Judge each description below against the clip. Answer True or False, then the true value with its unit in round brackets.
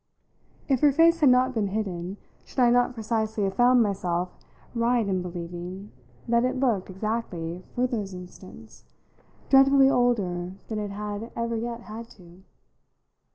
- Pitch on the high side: True (220 Hz)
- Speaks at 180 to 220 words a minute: False (150 wpm)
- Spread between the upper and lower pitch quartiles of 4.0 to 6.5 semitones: True (4.6 semitones)